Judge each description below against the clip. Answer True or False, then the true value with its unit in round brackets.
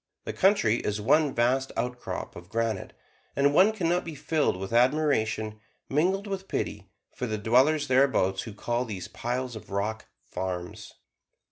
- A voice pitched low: True (125 Hz)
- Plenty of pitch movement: True (5.7 semitones)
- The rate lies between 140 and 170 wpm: True (160 wpm)